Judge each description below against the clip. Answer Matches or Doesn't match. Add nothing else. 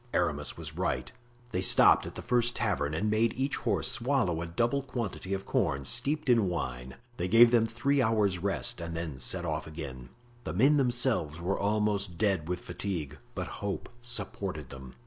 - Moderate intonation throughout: Doesn't match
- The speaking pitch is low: Matches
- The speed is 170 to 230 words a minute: Matches